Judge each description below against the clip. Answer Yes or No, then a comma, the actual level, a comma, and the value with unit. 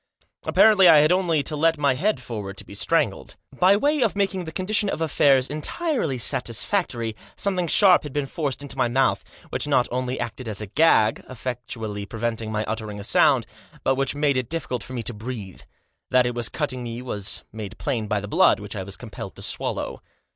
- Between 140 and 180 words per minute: No, fast, 205 wpm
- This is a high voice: No, low, 130 Hz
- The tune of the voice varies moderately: No, wide, 6.0 semitones